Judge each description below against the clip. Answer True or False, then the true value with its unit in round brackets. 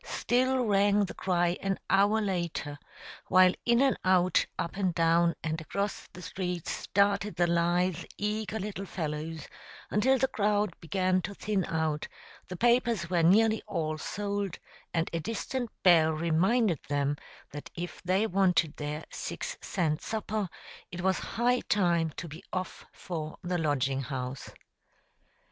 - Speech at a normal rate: True (145 wpm)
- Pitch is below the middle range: False (185 Hz)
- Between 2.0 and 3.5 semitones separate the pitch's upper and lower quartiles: False (3.9 semitones)